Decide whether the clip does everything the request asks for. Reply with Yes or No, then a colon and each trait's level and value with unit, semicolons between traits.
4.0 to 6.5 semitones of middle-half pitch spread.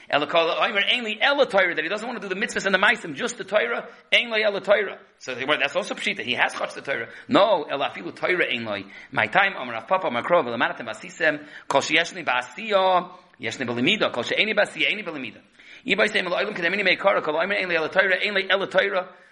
No: average, 3.2 semitones